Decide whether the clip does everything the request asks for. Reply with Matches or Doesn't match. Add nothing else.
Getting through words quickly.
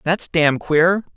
Doesn't match